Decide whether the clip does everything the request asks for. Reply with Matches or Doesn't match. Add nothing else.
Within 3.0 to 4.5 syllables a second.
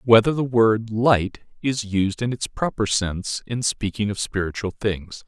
Matches